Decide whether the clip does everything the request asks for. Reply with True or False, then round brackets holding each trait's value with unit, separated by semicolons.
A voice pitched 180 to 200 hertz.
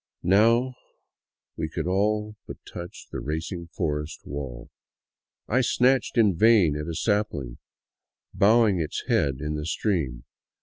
False (90 Hz)